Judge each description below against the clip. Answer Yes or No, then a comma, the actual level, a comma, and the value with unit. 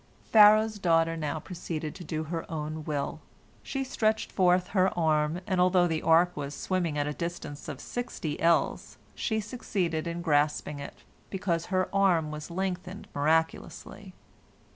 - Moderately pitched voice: Yes, medium, 170 Hz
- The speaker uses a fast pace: No, average, 150 wpm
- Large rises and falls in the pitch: No, average, 3.2 semitones